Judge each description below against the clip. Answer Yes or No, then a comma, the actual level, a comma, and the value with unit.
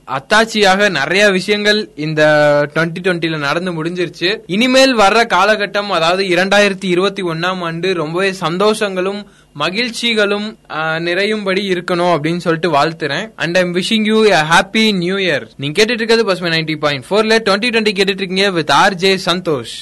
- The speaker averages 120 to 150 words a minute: Yes, average, 125 wpm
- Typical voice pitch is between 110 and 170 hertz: No, medium, 185 Hz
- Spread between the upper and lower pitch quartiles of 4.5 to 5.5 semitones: No, average, 3.8 semitones